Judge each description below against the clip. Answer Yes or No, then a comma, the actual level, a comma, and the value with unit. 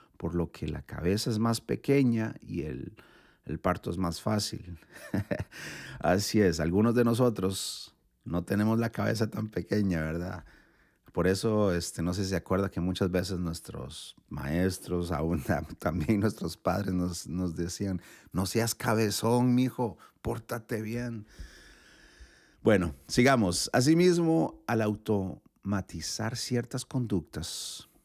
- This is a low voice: Yes, low, 100 Hz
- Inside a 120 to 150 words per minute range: Yes, average, 130 wpm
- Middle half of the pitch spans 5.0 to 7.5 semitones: No, average, 4.5 semitones